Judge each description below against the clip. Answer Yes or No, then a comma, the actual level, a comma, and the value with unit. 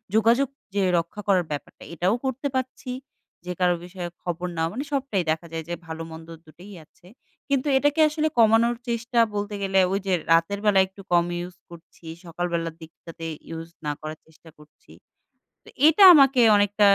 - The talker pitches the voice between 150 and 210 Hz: Yes, high, 190 Hz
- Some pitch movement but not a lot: No, wide, 5.8 semitones